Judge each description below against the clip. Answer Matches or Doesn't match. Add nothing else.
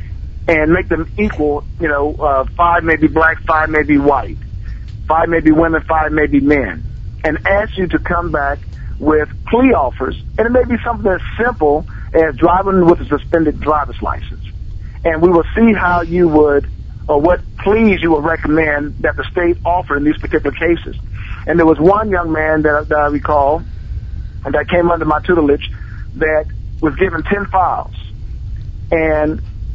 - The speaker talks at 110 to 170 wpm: Doesn't match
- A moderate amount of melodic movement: Matches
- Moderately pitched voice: Matches